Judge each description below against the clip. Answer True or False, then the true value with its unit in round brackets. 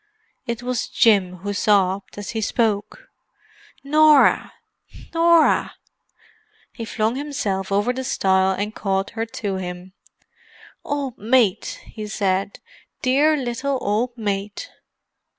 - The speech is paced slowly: True (115 wpm)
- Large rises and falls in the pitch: False (4.7 semitones)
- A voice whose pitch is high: True (220 Hz)